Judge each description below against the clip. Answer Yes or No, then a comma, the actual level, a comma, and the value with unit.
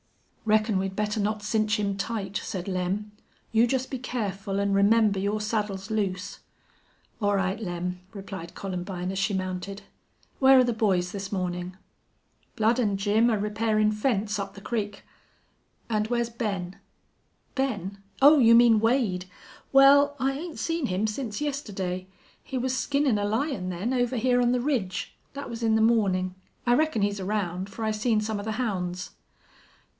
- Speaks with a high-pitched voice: Yes, high, 210 Hz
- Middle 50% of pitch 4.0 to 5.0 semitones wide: No, average, 3.4 semitones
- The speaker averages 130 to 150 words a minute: No, average, 165 wpm